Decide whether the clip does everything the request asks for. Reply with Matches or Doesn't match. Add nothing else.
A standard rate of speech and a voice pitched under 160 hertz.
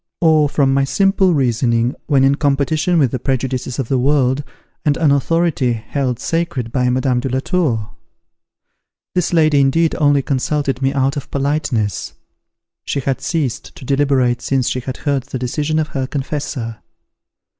Matches